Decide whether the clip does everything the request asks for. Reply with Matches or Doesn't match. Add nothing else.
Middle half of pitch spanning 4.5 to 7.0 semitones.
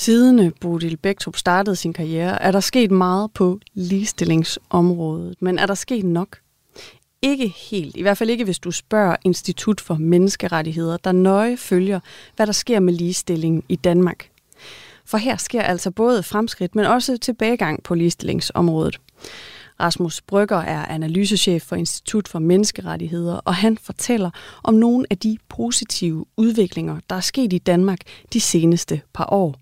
Doesn't match